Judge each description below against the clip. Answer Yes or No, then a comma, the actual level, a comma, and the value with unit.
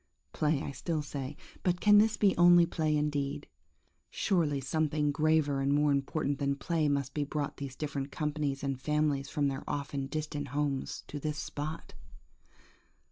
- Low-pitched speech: No, medium, 145 Hz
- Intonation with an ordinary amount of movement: No, narrow, 1.9 semitones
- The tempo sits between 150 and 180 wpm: Yes, average, 160 wpm